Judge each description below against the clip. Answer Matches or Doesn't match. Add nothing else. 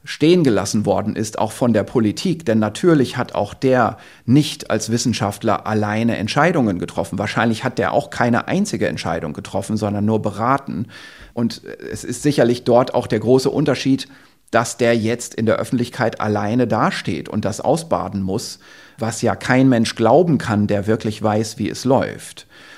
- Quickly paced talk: Doesn't match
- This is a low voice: Matches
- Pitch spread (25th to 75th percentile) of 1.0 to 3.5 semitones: Matches